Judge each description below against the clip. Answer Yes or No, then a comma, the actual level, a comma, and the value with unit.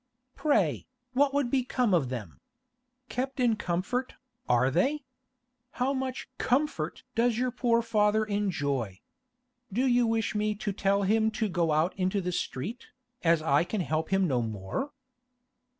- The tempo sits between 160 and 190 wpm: No, average, 150 wpm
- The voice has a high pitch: Yes, high, 210 Hz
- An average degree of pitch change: No, wide, 6.8 semitones